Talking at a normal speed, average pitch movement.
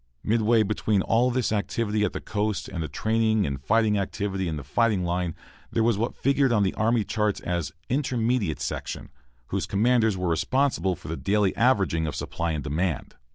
Yes: average, 185 wpm; average, 4.3 semitones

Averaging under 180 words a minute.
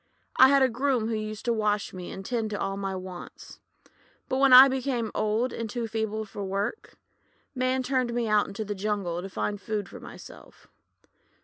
No: average, 195 wpm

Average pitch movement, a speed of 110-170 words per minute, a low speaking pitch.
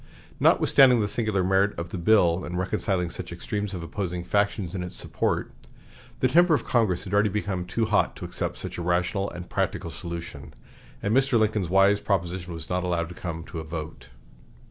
No: average, 3.2 semitones; average, 190 wpm; very low, 95 Hz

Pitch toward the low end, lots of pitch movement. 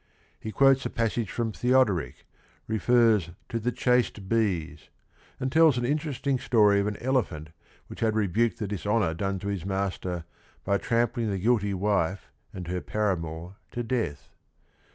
No: low, 105 Hz; average, 4.2 semitones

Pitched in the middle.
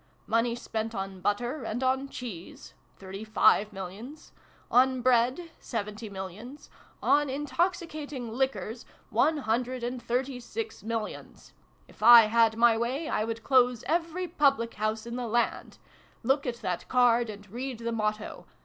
No: high, 240 Hz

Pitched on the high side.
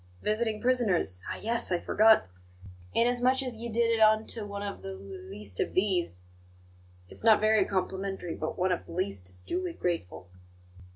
Yes: high, 195 Hz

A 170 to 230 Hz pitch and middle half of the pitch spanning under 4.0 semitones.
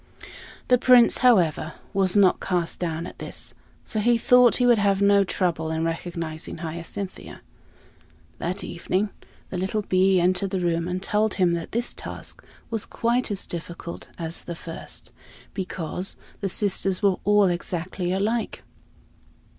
Yes: medium, 185 Hz; average, 3.3 semitones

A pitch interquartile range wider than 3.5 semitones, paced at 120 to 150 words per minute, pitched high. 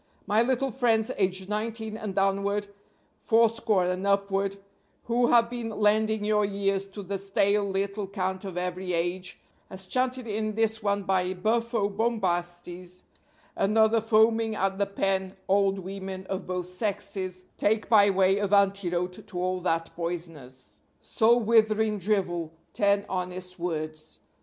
No: average, 2.8 semitones; average, 140 wpm; high, 200 Hz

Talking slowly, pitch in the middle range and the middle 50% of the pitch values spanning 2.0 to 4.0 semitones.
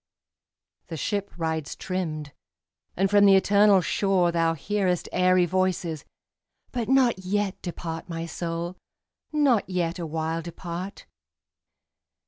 Yes: slow, 110 wpm; medium, 180 Hz; average, 3.0 semitones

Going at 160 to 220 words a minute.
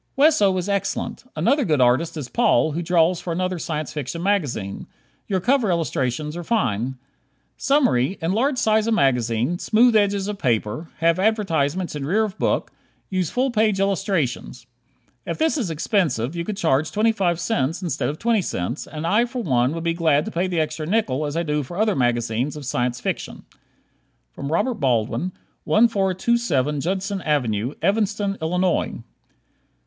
Yes: average, 165 wpm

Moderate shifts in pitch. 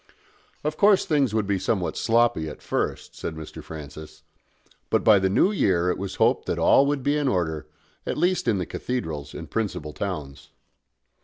No: wide, 8.2 semitones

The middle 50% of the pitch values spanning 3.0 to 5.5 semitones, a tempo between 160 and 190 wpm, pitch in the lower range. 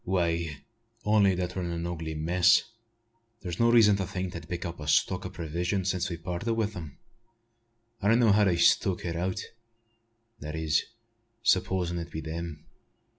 No: narrow, 2.5 semitones; average, 180 wpm; very low, 90 Hz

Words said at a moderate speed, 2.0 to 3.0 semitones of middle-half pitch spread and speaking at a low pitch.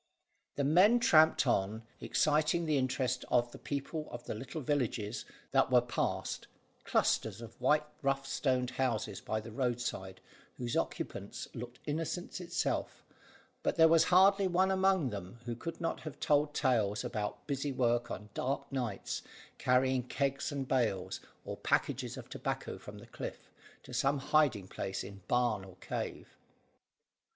No: average, 150 wpm; average, 4.3 semitones; low, 130 Hz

